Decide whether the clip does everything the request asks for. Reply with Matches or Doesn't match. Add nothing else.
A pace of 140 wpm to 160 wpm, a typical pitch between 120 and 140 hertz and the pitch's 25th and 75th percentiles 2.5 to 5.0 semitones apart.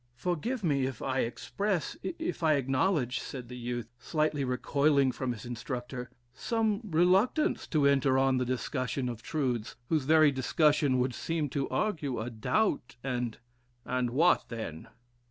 Matches